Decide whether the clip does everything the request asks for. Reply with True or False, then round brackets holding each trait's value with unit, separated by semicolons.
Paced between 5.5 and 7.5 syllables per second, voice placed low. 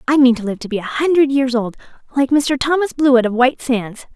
False (5.9 syllables/s; 260 Hz)